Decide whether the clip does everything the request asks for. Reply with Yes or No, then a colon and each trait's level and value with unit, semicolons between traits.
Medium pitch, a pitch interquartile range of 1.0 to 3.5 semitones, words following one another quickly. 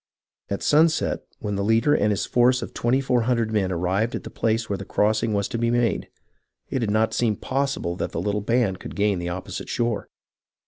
No: low, 110 Hz; average, 3.2 semitones; fast, 220 wpm